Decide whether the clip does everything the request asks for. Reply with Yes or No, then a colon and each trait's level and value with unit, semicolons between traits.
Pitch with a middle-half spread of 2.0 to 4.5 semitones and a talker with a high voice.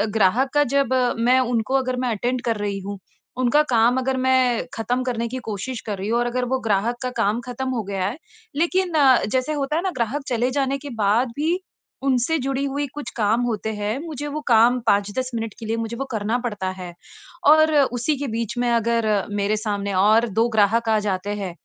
Yes: average, 3.4 semitones; high, 235 Hz